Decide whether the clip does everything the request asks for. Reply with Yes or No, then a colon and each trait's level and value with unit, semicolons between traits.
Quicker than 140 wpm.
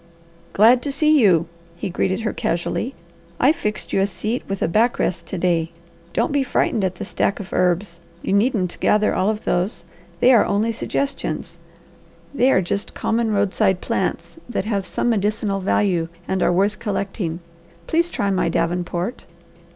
Yes: average, 170 wpm